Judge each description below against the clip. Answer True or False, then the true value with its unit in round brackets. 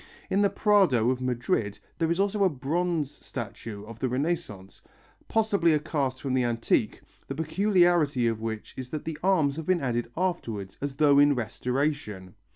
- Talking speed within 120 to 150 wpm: False (170 wpm)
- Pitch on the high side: False (140 Hz)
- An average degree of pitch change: False (6.2 semitones)